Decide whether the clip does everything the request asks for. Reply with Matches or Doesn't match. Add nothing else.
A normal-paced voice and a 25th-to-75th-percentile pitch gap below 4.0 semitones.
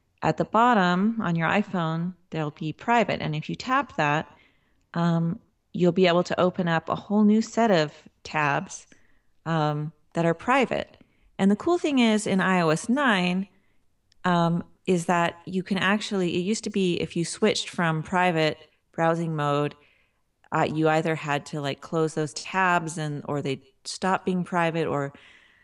Matches